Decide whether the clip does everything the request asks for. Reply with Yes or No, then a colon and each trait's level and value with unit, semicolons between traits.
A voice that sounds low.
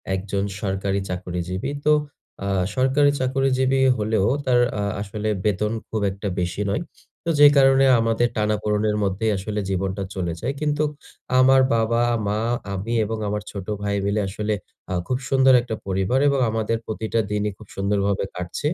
Yes: low, 105 Hz